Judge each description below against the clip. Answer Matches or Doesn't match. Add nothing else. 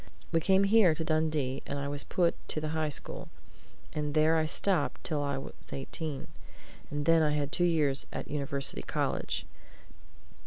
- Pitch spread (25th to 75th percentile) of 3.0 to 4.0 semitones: Doesn't match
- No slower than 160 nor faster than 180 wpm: Matches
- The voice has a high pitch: Doesn't match